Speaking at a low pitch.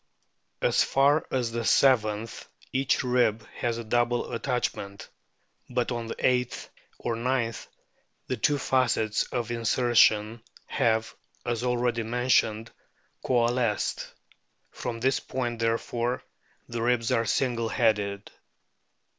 Yes: low, 120 Hz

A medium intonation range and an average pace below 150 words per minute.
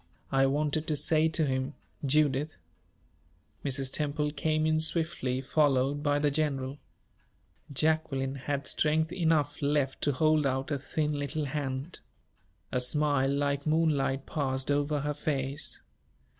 No: narrow, 2.3 semitones; slow, 135 wpm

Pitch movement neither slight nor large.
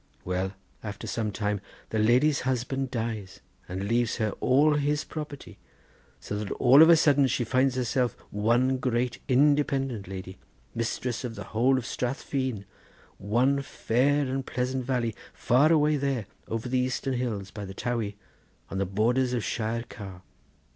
Yes: average, 3.7 semitones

